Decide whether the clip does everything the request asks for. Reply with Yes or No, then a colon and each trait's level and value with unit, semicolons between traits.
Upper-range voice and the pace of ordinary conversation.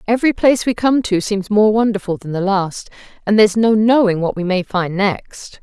No: high, 205 Hz; fast, 215 wpm